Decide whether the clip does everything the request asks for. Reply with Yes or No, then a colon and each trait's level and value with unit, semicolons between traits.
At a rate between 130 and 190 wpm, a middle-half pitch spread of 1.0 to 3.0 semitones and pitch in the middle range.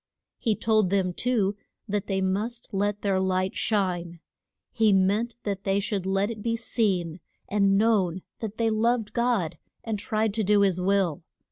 No: average, 165 wpm; narrow, 2.6 semitones; high, 200 Hz